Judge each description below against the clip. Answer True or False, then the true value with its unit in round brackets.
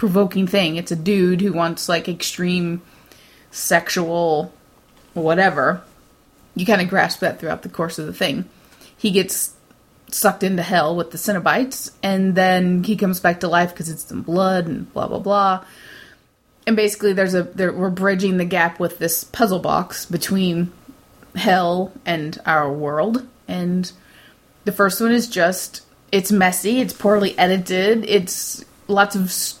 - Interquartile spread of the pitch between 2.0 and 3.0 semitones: True (2.5 semitones)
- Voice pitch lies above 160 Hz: True (185 Hz)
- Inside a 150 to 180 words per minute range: True (155 wpm)